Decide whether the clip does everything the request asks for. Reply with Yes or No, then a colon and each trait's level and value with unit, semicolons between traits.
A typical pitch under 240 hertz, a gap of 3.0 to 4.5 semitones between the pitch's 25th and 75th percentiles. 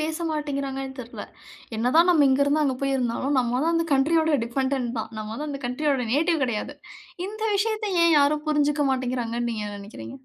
No: very high, 275 Hz; average, 3.7 semitones